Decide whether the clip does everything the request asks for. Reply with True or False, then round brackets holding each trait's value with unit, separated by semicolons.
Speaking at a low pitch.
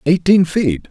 False (165 Hz)